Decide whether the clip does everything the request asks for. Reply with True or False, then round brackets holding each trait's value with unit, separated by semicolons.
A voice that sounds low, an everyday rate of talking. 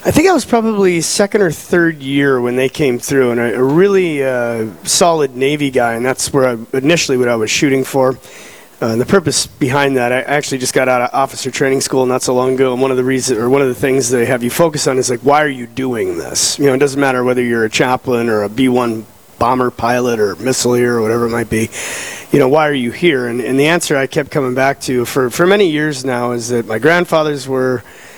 False (130 Hz; 255 wpm)